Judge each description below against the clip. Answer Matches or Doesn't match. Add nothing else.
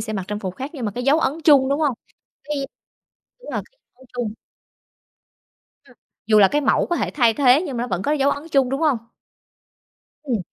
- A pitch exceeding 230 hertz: Matches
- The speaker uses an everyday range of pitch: Matches